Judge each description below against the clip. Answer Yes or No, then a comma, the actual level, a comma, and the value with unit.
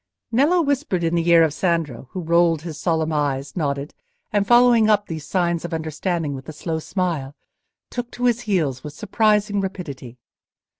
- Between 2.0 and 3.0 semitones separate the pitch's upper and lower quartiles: No, average, 5.3 semitones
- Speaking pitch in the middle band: Yes, medium, 170 Hz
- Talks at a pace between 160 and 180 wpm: Yes, average, 170 wpm